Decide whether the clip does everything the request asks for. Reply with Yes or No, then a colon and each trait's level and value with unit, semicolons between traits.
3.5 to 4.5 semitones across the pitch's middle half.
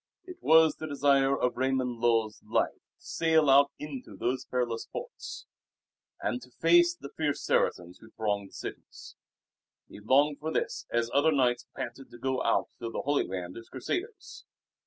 Yes: average, 4.1 semitones